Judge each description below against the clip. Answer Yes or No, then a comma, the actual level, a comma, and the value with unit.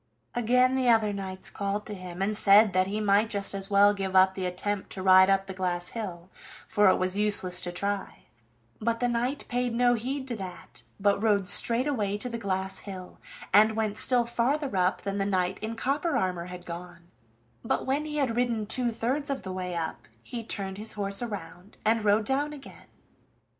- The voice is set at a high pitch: Yes, high, 205 Hz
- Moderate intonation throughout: Yes, average, 3.8 semitones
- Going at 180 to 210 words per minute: Yes, fast, 205 wpm